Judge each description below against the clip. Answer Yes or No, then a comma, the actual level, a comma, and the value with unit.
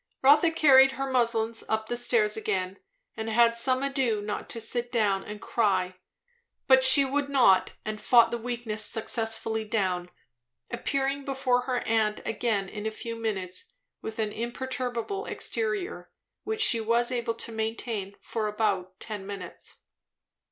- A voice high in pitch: Yes, high, 230 Hz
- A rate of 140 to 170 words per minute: Yes, average, 145 wpm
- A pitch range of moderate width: Yes, average, 3.3 semitones